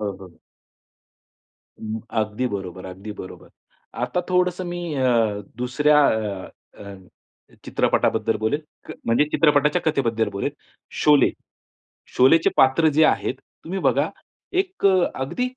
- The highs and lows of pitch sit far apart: Yes, wide, 6.7 semitones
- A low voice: Yes, low, 130 Hz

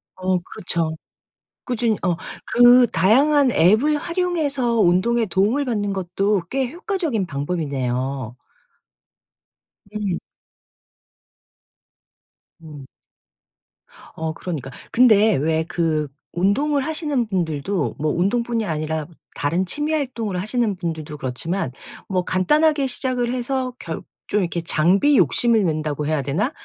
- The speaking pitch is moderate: No, high, 195 Hz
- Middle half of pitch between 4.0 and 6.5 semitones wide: No, wide, 7.5 semitones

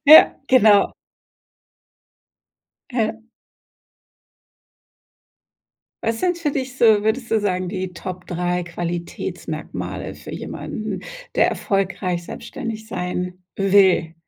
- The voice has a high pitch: Yes, high, 195 Hz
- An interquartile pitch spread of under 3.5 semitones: No, average, 4.1 semitones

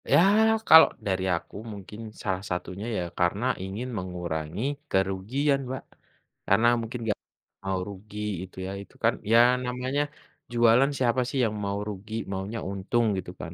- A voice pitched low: Yes, low, 100 Hz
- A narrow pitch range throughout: No, average, 3.9 semitones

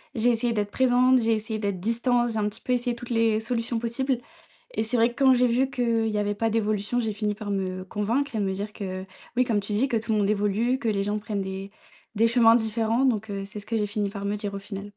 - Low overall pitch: No, high, 220 Hz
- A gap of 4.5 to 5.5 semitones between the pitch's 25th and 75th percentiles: No, narrow, 2.6 semitones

